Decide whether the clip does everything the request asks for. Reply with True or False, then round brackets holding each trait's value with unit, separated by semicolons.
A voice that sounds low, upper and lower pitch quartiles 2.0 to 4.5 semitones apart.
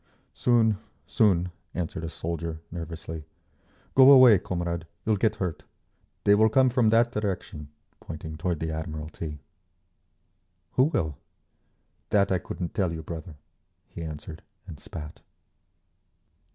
False (85 Hz; 5.0 semitones)